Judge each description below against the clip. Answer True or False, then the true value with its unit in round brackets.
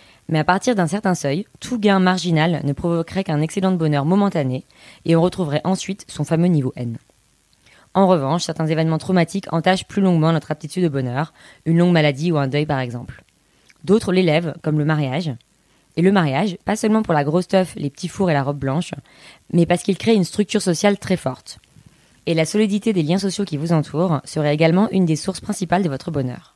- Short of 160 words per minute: False (210 wpm)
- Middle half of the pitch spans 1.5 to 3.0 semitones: False (3.9 semitones)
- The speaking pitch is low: False (170 Hz)